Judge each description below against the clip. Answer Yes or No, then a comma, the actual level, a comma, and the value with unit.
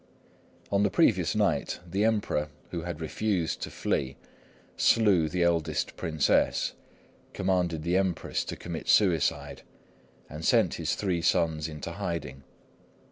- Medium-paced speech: No, slow, 130 wpm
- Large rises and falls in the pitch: No, average, 3.1 semitones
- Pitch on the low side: Yes, very low, 85 Hz